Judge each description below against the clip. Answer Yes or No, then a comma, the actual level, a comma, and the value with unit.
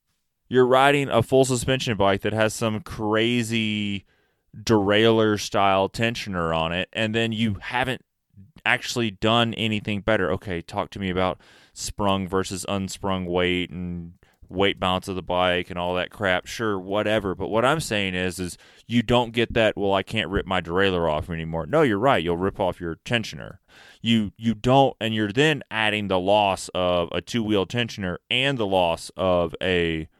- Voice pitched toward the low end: Yes, low, 100 Hz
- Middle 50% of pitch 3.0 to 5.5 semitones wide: Yes, average, 3.6 semitones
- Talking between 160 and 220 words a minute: Yes, average, 175 wpm